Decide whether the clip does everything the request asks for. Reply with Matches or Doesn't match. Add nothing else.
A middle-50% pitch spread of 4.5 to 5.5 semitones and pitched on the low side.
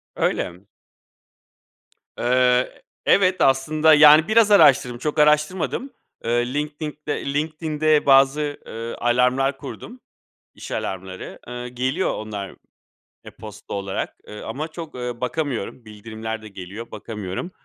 Matches